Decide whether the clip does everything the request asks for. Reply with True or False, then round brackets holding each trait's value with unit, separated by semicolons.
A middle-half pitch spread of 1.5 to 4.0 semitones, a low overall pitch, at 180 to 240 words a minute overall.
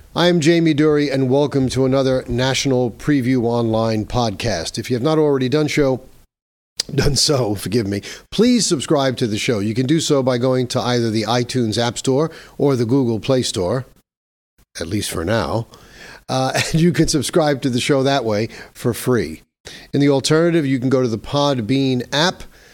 True (3.4 semitones; 130 Hz; 185 wpm)